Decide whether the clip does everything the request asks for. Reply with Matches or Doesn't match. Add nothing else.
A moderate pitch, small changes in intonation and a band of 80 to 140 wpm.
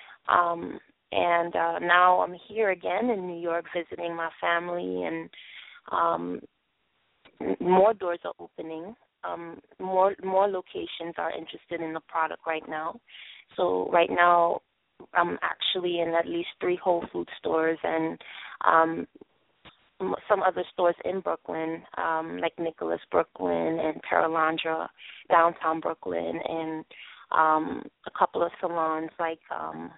Matches